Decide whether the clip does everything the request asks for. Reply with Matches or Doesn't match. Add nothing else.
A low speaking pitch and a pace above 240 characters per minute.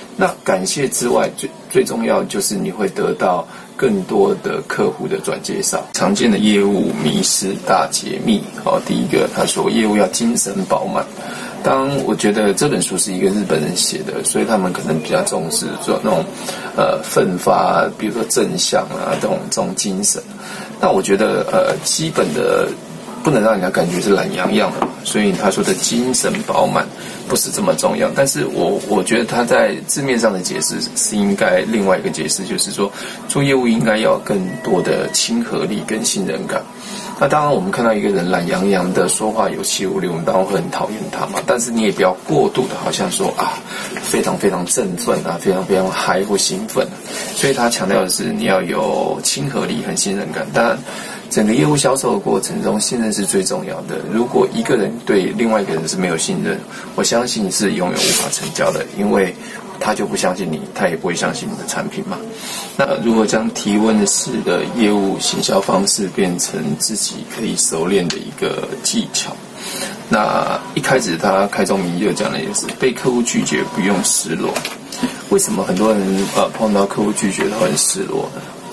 Matches